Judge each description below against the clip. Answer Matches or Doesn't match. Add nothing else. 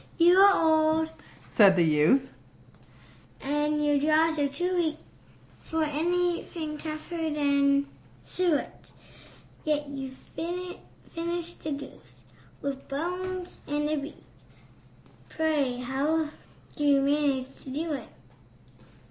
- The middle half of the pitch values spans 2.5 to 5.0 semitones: Matches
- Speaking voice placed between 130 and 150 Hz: Doesn't match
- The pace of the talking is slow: Matches